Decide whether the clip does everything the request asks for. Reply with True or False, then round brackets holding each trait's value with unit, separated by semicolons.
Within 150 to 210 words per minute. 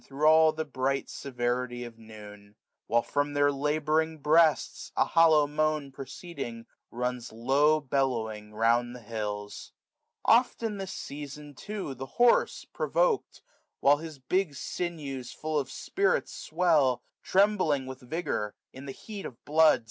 False (140 wpm)